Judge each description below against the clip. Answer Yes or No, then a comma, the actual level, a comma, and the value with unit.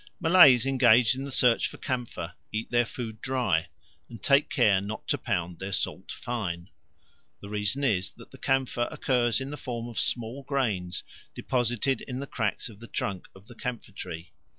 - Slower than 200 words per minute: Yes, average, 180 wpm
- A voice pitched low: Yes, low, 120 Hz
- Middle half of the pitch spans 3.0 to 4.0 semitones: No, average, 4.5 semitones